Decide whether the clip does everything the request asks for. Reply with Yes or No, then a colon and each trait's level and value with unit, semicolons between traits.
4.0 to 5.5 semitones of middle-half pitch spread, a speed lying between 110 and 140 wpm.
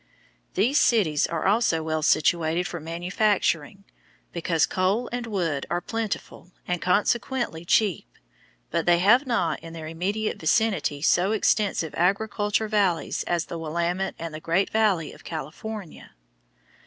Yes: average, 4.5 semitones; slow, 135 wpm